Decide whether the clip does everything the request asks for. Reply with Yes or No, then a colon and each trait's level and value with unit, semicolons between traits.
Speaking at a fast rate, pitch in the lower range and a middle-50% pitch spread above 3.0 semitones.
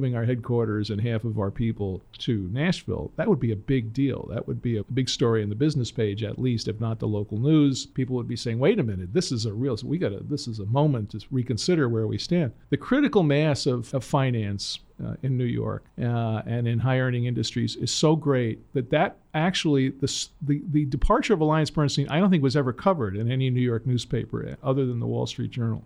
Yes: fast, 230 wpm; low, 125 Hz; average, 4.2 semitones